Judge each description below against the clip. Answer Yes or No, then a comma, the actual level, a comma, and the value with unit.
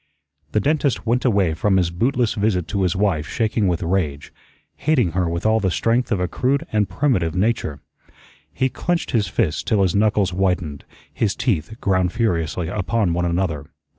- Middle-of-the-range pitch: No, very low, 95 Hz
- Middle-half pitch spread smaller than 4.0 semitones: No, average, 4.5 semitones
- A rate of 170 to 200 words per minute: Yes, average, 175 wpm